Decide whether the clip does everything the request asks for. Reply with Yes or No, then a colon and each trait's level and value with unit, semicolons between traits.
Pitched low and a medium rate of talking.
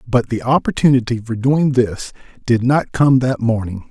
Yes: low, 120 Hz; average, 170 wpm